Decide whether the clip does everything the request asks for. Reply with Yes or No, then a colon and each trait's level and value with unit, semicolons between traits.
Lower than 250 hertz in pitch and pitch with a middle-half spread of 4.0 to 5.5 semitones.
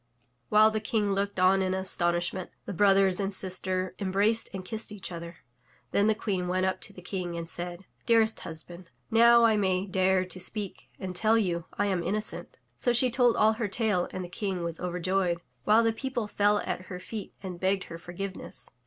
No: high, 190 Hz; average, 2.8 semitones